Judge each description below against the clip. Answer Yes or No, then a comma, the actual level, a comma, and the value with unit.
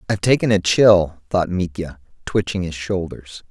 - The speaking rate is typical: Yes, average, 155 wpm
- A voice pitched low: Yes, very low, 90 Hz